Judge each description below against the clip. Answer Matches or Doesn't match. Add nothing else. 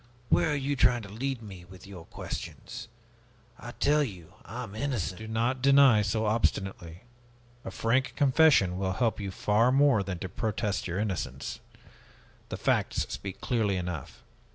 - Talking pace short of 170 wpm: Matches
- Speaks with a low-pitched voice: Matches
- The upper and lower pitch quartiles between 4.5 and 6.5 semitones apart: Matches